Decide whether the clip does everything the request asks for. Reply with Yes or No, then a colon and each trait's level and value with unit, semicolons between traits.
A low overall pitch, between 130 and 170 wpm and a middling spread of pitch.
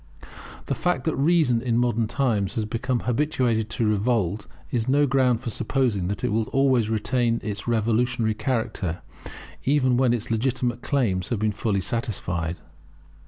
Yes: low, 115 Hz; average, 155 wpm; average, 3.1 semitones